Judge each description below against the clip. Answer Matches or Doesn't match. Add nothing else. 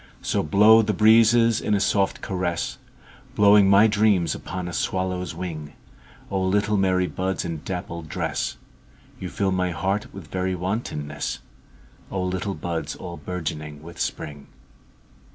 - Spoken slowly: Matches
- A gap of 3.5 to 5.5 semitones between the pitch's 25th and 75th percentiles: Doesn't match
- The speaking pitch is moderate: Doesn't match